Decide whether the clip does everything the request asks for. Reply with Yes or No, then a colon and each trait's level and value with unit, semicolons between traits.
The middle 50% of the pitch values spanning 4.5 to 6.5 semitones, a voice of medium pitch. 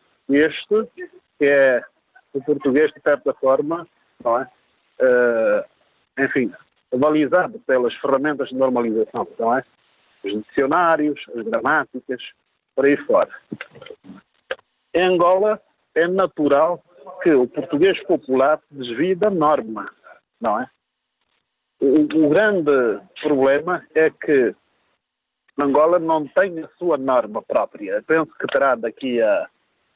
Yes: average, 4.9 semitones; medium, 150 Hz